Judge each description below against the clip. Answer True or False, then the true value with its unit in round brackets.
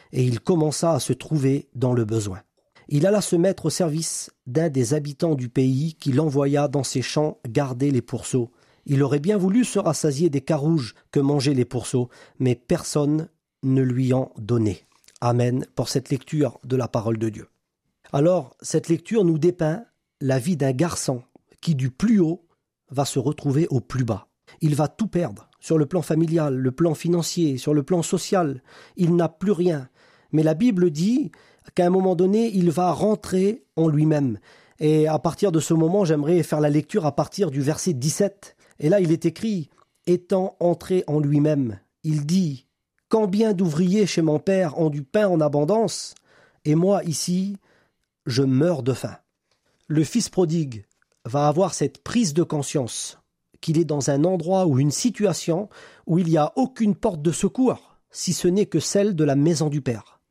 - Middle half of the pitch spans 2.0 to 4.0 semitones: False (4.5 semitones)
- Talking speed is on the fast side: False (185 wpm)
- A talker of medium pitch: True (155 Hz)